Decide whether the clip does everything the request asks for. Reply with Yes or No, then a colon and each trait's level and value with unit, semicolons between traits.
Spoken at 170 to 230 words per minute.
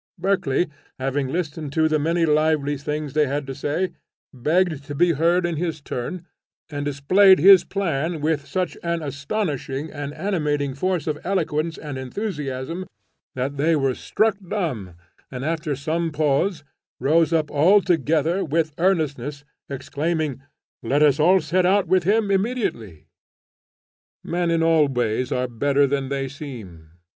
No: average, 145 wpm